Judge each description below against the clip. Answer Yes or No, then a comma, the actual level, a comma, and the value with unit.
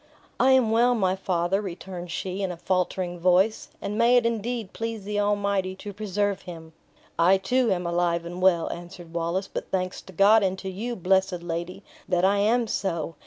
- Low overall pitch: No, high, 190 Hz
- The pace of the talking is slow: No, average, 190 wpm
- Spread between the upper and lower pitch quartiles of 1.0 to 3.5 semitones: Yes, average, 2.8 semitones